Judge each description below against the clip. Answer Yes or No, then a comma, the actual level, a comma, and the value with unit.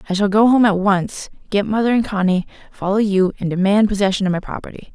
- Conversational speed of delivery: No, fast, 220 wpm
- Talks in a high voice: Yes, high, 200 Hz